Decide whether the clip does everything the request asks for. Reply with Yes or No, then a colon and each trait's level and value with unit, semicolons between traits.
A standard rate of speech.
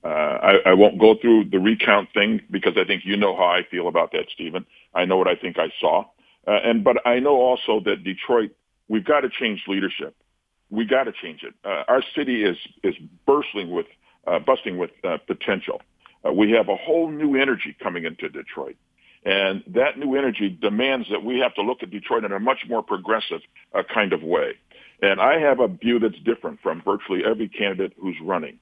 No: fast, 210 wpm